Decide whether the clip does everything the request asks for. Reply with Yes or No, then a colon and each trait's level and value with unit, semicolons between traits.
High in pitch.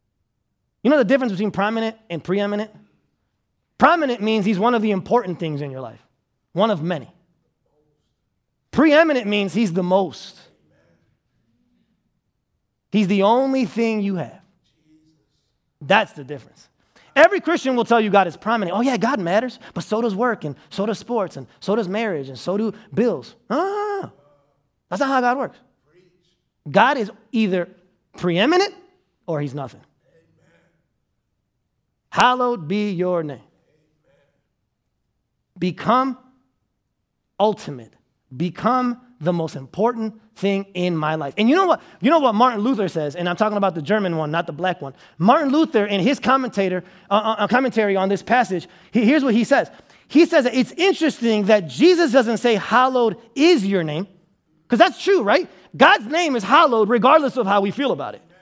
Yes: high, 210 Hz